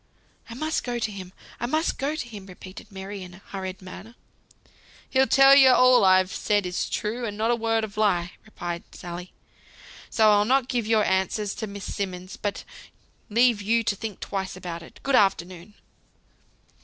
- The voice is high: Yes, high, 205 Hz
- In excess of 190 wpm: No, average, 180 wpm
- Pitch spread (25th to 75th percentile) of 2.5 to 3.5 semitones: No, average, 3.9 semitones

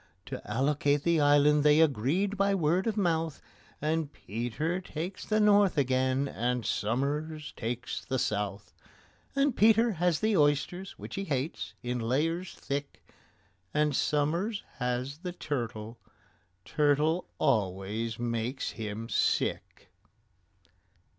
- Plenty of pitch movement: Yes, wide, 5.8 semitones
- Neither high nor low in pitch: Yes, medium, 145 Hz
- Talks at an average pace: No, slow, 115 wpm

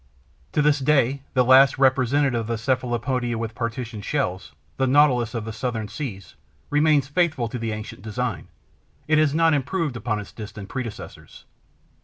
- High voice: No, low, 125 Hz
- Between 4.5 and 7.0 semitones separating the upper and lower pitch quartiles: No, average, 3.8 semitones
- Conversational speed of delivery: Yes, average, 160 wpm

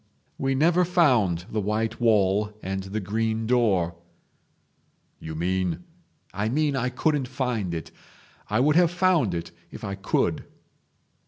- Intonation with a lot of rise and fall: Yes, wide, 5.8 semitones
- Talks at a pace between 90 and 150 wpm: Yes, average, 145 wpm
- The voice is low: Yes, low, 110 Hz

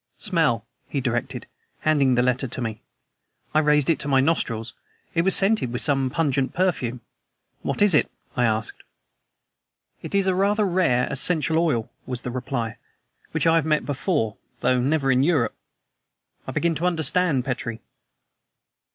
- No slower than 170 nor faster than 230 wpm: No, average, 160 wpm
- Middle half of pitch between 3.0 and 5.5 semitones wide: Yes, average, 5.1 semitones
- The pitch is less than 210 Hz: Yes, medium, 140 Hz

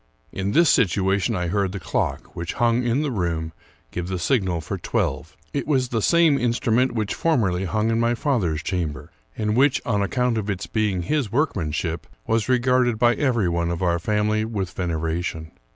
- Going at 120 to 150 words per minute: No, average, 185 wpm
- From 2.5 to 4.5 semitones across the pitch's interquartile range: No, wide, 5.6 semitones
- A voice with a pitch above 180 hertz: No, low, 105 Hz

